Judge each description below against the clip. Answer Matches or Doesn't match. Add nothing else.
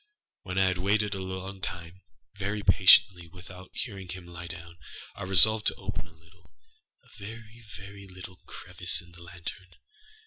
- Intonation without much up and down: Matches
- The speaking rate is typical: Matches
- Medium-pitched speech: Doesn't match